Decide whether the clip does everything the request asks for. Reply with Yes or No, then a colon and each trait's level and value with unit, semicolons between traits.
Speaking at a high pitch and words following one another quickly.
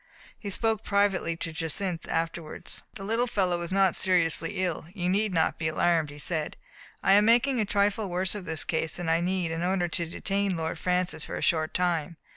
No: medium, 180 Hz; fast, 210 wpm